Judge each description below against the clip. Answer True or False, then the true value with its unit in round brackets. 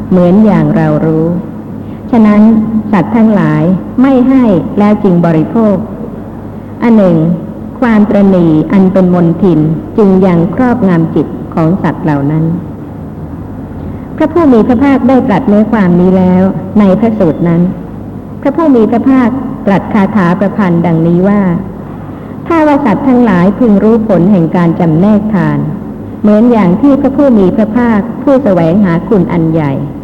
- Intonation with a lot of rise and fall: False (4.7 semitones)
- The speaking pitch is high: True (200 Hz)